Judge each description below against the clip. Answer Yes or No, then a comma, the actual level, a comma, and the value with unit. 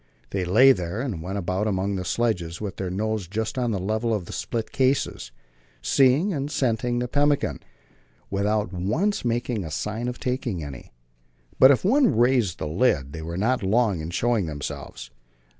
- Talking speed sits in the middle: Yes, average, 175 wpm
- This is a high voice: No, low, 110 Hz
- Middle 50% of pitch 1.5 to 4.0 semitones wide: No, average, 5.3 semitones